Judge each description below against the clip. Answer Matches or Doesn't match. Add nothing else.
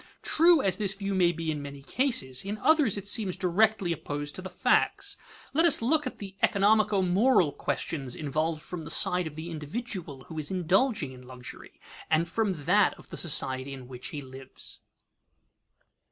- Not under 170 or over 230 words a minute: Matches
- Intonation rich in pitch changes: Matches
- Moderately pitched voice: Matches